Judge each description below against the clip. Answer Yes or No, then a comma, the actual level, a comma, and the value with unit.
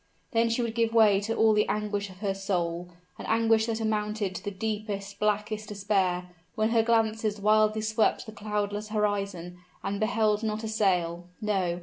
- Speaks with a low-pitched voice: No, high, 210 Hz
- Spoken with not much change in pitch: Yes, narrow, 1.8 semitones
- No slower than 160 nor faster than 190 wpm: Yes, average, 180 wpm